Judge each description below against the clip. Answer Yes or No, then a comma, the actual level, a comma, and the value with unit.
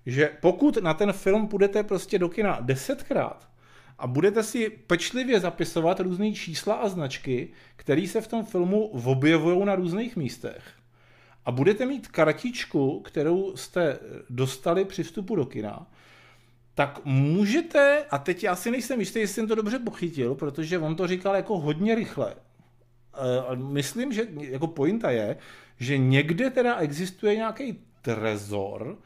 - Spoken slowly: No, average, 145 wpm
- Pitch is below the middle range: No, medium, 175 Hz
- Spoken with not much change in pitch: No, wide, 7.8 semitones